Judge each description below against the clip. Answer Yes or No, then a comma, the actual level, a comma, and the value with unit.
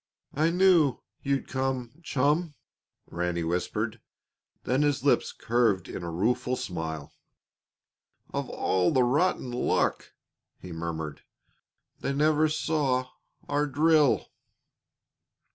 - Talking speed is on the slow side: Yes, slow, 105 wpm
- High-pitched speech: No, low, 130 Hz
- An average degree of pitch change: No, wide, 8.3 semitones